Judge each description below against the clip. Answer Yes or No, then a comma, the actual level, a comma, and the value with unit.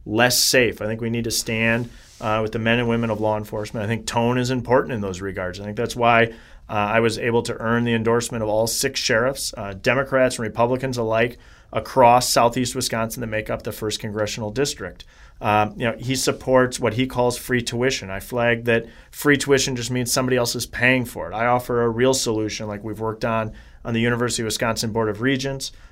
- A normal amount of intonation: No, narrow, 2.2 semitones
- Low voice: Yes, low, 115 Hz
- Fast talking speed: Yes, fast, 220 wpm